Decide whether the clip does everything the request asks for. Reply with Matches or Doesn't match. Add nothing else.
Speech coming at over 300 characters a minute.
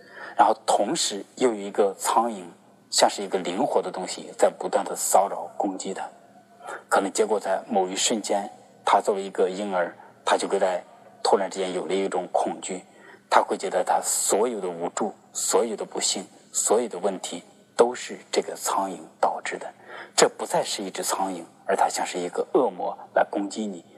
Doesn't match